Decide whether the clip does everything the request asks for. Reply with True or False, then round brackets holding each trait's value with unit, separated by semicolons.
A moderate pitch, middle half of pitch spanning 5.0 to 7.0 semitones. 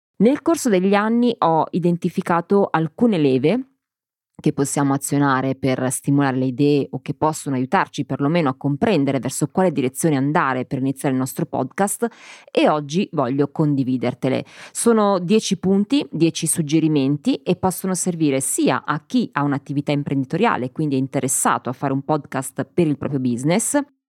True (150 Hz; 5.4 semitones)